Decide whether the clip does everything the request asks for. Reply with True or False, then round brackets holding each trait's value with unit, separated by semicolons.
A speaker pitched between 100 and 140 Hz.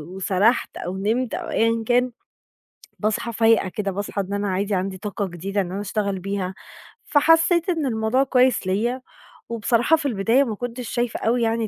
False (220 Hz)